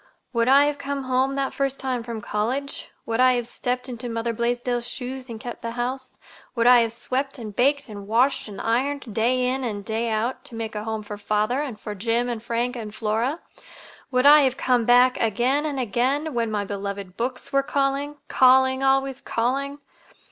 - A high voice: Yes, high, 245 Hz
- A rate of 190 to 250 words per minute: Yes, average, 200 wpm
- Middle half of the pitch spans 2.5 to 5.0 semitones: Yes, average, 2.9 semitones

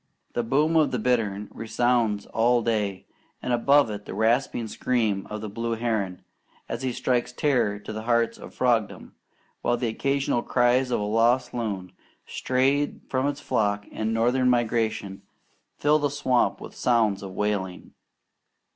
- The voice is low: Yes, low, 115 Hz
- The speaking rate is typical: Yes, average, 155 wpm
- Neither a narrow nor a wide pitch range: Yes, average, 3.0 semitones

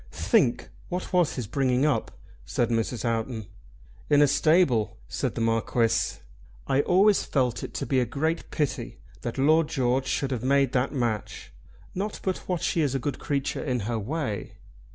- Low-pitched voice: Yes, low, 130 Hz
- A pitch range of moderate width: Yes, average, 4.2 semitones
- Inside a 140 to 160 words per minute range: No, average, 175 wpm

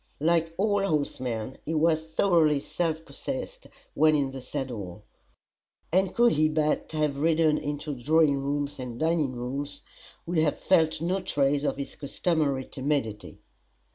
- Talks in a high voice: No, medium, 150 Hz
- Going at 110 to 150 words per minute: Yes, average, 140 wpm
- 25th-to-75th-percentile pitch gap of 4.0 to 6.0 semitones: No, average, 2.8 semitones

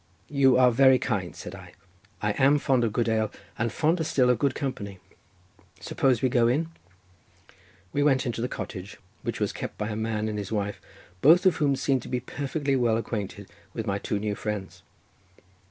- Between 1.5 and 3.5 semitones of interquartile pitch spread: No, average, 4.4 semitones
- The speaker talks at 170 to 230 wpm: Yes, average, 185 wpm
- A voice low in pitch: Yes, low, 115 Hz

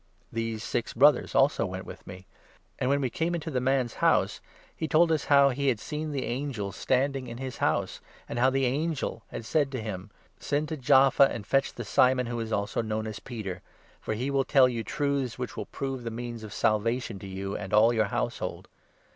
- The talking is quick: Yes, fast, 225 wpm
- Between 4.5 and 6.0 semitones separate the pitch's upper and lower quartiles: No, average, 3.8 semitones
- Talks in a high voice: No, low, 125 Hz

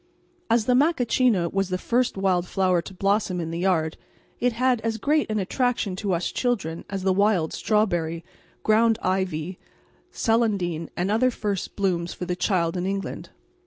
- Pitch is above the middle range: Yes, high, 195 Hz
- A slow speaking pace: No, average, 165 wpm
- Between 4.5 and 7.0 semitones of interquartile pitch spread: No, average, 4.0 semitones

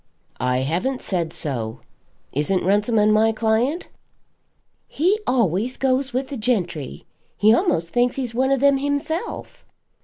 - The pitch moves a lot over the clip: Yes, wide, 7.0 semitones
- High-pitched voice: Yes, high, 225 Hz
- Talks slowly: Yes, slow, 130 wpm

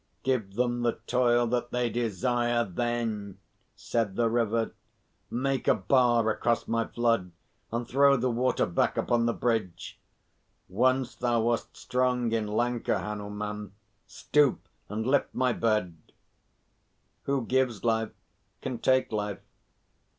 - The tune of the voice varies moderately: No, narrow, 2.1 semitones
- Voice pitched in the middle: No, low, 120 Hz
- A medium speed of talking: No, slow, 130 wpm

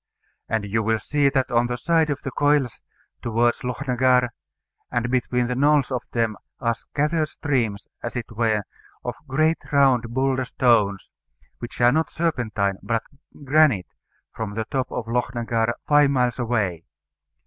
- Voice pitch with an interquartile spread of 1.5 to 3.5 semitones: Yes, average, 3.2 semitones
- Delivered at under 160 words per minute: Yes, average, 150 wpm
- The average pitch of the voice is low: Yes, low, 125 Hz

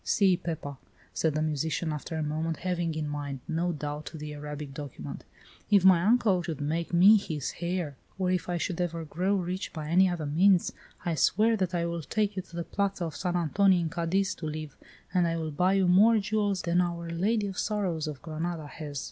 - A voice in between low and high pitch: Yes, medium, 170 Hz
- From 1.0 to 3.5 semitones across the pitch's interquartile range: Yes, average, 3.2 semitones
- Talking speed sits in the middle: No, fast, 210 wpm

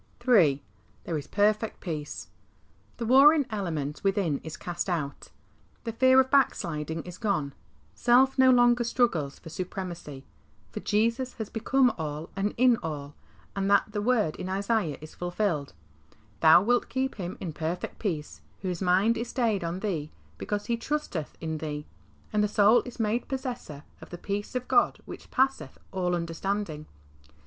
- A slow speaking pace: No, average, 155 wpm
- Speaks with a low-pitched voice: No, high, 195 Hz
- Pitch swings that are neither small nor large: No, wide, 6.5 semitones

